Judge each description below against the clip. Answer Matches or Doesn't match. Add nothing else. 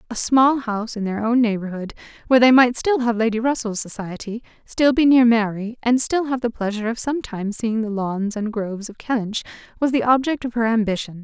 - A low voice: Doesn't match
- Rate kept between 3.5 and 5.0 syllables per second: Doesn't match